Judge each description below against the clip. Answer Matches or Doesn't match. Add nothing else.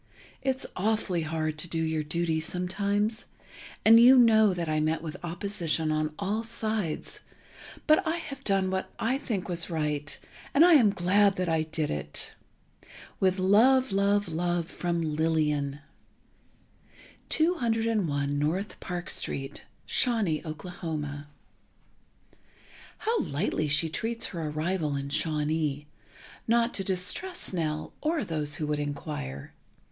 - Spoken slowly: Matches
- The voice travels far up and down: Matches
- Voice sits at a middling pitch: Matches